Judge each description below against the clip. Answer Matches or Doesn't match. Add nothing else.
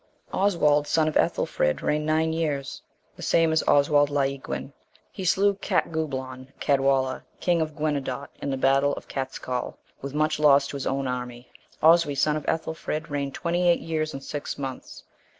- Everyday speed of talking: Matches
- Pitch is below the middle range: Doesn't match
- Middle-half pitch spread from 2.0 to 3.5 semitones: Matches